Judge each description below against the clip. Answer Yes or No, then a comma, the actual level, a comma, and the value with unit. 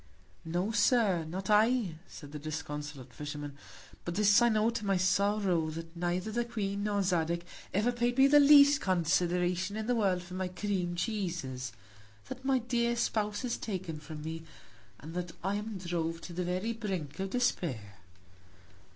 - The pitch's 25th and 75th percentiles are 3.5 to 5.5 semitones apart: Yes, average, 4.6 semitones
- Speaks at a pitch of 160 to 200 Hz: Yes, medium, 185 Hz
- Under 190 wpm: Yes, average, 170 wpm